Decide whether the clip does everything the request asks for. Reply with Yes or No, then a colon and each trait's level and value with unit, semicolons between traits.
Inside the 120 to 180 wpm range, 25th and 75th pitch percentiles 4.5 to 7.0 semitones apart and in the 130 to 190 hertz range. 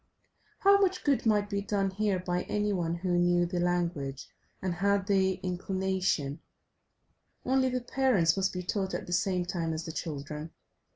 No: average, 170 wpm; average, 2.7 semitones; medium, 185 Hz